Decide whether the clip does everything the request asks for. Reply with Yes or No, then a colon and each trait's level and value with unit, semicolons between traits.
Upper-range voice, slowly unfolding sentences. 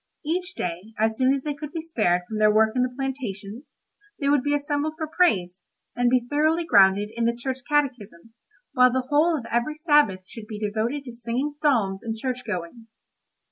No: very high, 250 Hz; average, 195 wpm